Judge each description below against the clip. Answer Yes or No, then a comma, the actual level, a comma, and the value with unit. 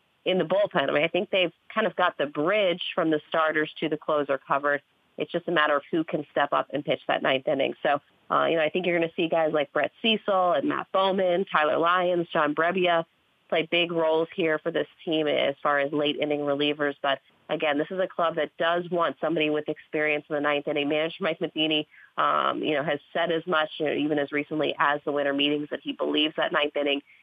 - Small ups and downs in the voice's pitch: Yes, narrow, 2.3 semitones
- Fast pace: Yes, fast, 240 wpm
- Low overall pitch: No, medium, 155 Hz